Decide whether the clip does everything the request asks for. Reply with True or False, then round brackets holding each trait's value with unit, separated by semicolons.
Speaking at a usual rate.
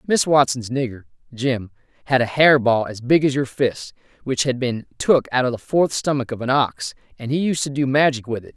False (230 wpm)